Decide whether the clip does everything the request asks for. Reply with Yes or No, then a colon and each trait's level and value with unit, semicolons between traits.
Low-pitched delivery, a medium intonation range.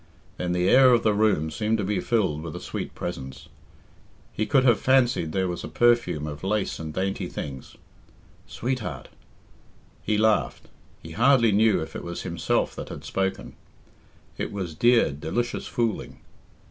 No: low, 100 Hz; wide, 6.2 semitones